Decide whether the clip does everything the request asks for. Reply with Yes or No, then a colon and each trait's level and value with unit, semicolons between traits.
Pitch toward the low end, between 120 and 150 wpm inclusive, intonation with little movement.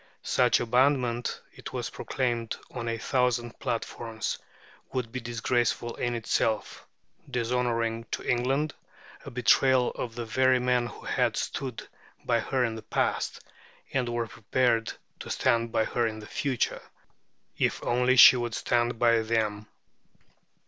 Yes: low, 120 Hz; average, 140 wpm; narrow, 1.5 semitones